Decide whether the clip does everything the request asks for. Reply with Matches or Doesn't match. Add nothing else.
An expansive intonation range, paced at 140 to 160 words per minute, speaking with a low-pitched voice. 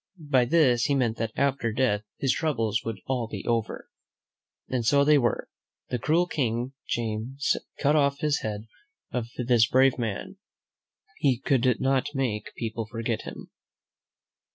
Doesn't match